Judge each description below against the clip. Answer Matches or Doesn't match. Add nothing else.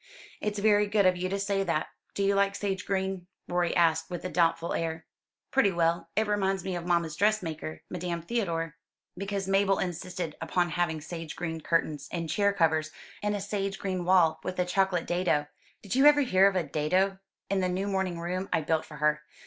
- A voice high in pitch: Doesn't match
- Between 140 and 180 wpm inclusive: Doesn't match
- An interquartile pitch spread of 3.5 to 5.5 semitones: Doesn't match